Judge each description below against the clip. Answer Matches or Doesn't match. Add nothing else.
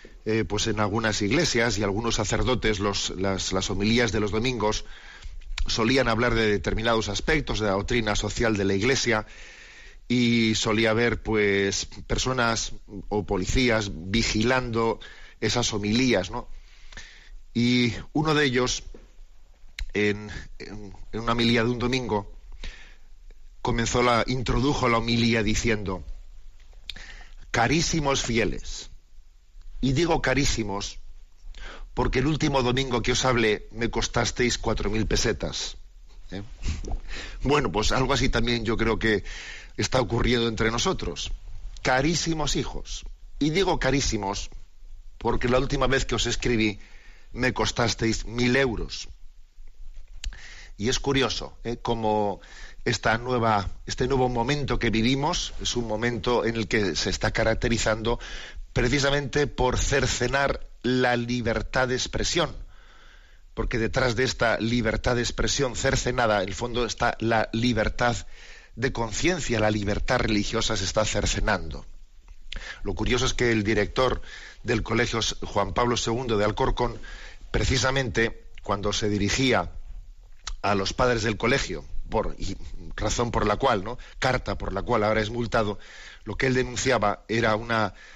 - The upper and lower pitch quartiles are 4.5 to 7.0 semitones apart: Doesn't match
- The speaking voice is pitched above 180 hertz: Doesn't match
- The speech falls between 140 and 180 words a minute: Doesn't match